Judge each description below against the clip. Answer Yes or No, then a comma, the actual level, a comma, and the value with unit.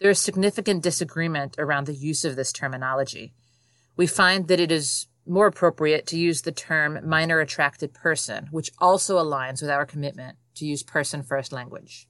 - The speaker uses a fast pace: No, average, 175 wpm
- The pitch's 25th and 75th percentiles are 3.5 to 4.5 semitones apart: Yes, average, 3.8 semitones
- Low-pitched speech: No, medium, 150 Hz